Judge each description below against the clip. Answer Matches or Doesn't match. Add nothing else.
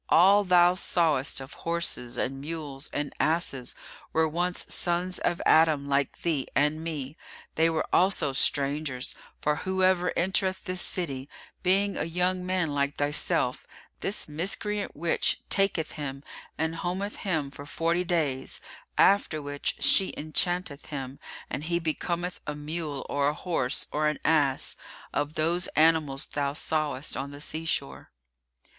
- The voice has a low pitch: Doesn't match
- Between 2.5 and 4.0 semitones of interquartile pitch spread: Matches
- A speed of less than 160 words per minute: Matches